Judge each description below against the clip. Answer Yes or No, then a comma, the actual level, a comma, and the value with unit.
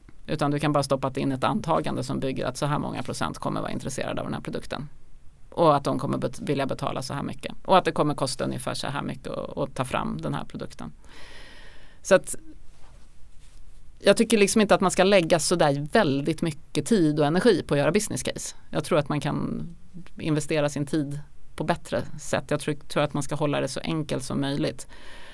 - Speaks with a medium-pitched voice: Yes, medium, 150 Hz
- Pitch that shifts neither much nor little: Yes, average, 3.7 semitones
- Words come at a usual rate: No, fast, 215 wpm